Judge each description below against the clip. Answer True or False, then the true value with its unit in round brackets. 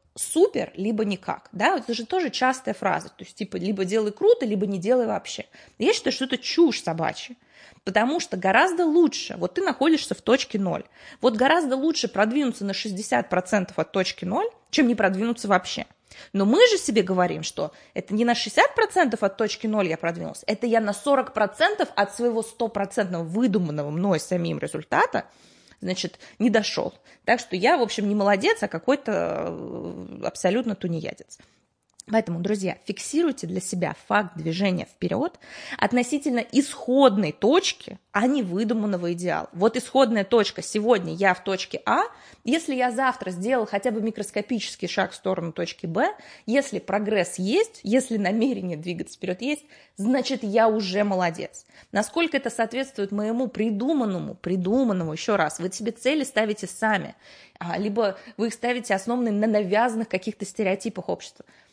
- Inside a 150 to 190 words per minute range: True (155 wpm)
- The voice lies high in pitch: True (220 Hz)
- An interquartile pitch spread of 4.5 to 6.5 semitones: True (4.8 semitones)